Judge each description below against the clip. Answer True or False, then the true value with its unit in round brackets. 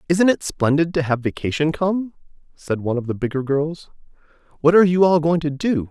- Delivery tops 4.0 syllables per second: True (5.6 syllables/s)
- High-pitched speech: False (155 Hz)